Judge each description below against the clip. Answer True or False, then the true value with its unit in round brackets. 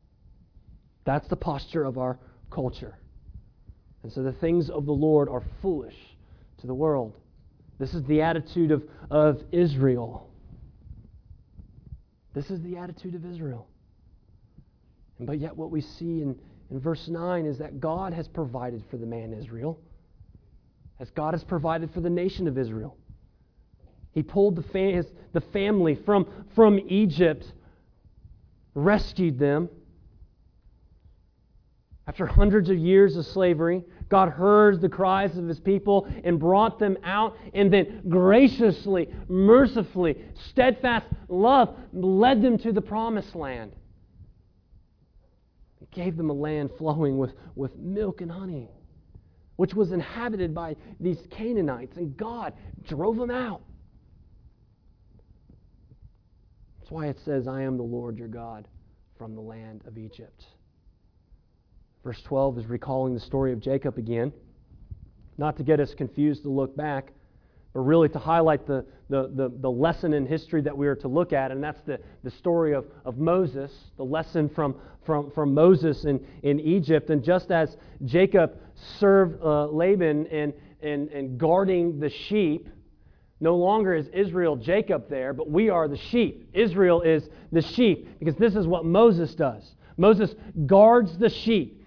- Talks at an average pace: True (145 wpm)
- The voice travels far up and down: True (7.0 semitones)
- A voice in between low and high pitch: True (150 Hz)